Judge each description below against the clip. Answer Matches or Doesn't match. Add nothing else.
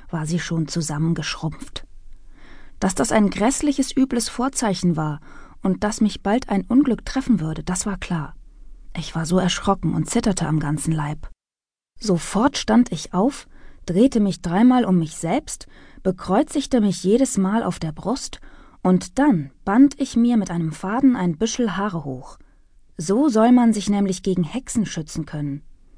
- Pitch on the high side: Matches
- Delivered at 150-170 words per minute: Matches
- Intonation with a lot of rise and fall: Matches